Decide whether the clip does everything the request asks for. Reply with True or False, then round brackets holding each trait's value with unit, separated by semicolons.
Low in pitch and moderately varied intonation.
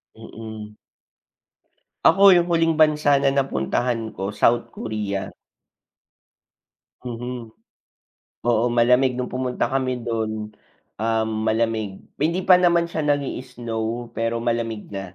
True (120 Hz; 3.8 semitones)